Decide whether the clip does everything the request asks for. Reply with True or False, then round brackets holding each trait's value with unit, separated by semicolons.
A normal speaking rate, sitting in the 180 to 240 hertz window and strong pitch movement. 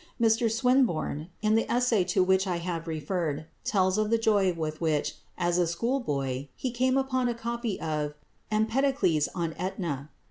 True (165 wpm; 190 Hz; 6.3 semitones)